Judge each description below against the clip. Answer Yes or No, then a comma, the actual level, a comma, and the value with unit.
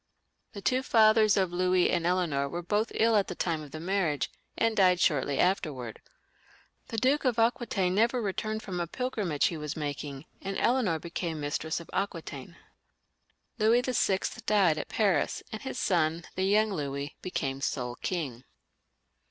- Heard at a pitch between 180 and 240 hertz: Yes, medium, 185 Hz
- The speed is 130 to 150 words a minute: No, average, 170 wpm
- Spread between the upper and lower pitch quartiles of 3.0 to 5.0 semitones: No, wide, 5.5 semitones